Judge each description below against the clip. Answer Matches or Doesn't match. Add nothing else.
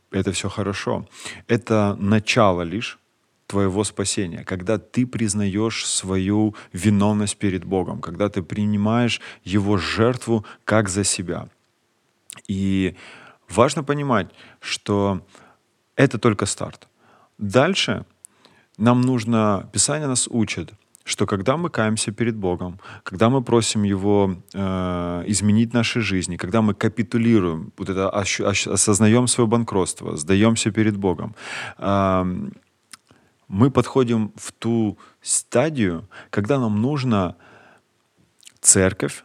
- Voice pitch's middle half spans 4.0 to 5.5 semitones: Doesn't match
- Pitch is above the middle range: Doesn't match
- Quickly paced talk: Doesn't match